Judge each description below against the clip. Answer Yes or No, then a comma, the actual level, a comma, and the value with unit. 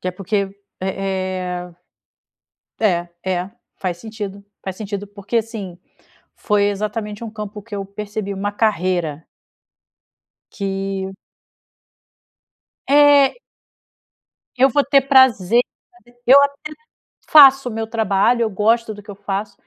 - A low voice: No, high, 205 Hz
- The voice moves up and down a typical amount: Yes, average, 3.0 semitones